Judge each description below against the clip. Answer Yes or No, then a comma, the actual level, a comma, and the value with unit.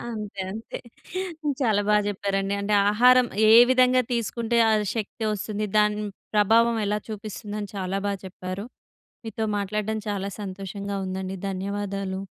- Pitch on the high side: Yes, high, 205 Hz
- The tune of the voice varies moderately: No, narrow, 1.9 semitones